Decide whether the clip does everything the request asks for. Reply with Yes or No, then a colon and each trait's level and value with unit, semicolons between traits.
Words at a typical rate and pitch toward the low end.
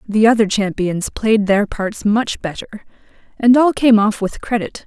No: average, 175 wpm; high, 215 Hz